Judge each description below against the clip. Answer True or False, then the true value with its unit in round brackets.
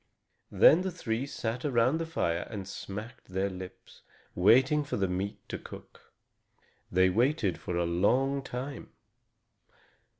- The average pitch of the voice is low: True (115 Hz)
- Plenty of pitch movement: True (6.6 semitones)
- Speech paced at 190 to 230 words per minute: False (135 wpm)